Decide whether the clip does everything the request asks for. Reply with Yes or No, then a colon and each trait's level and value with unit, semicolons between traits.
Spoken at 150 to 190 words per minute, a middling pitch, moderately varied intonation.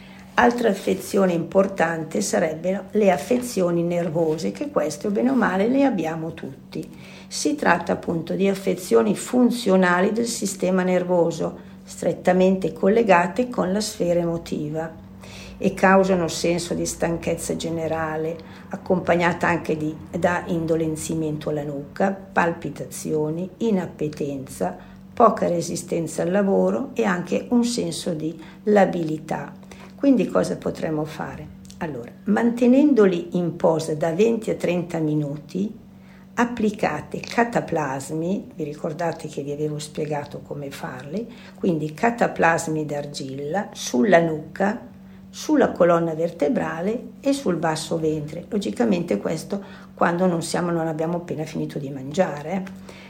No: average, 120 wpm; medium, 175 Hz; average, 3.6 semitones